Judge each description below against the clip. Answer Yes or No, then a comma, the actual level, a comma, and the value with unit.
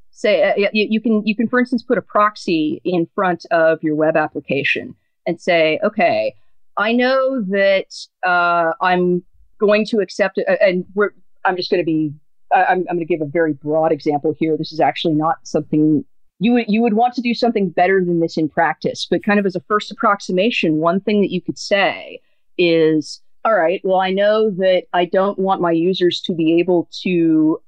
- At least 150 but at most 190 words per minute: No, average, 200 wpm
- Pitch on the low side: No, medium, 185 Hz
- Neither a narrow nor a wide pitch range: Yes, average, 4.2 semitones